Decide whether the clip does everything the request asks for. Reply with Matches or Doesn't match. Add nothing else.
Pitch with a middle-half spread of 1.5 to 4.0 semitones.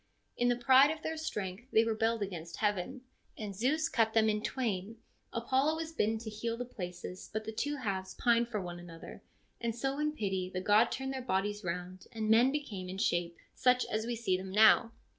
Doesn't match